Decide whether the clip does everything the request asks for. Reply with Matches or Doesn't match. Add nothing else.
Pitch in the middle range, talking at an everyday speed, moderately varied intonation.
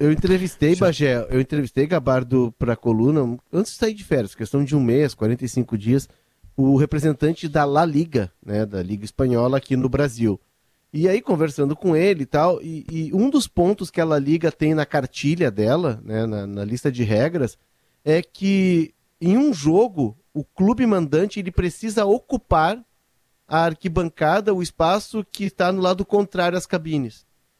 Doesn't match